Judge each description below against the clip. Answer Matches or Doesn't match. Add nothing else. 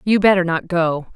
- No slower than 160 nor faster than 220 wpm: Matches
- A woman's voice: Matches